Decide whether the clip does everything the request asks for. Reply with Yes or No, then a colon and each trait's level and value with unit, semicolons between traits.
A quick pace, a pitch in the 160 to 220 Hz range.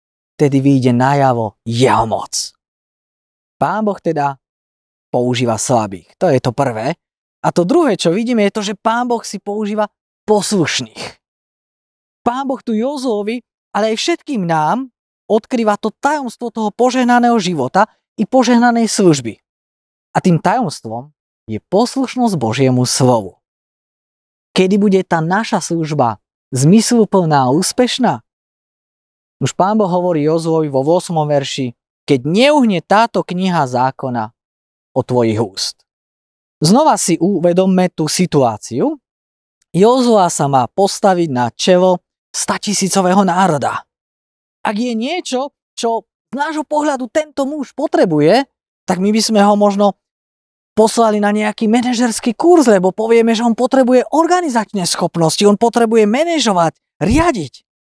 No: average, 125 wpm; high, 190 Hz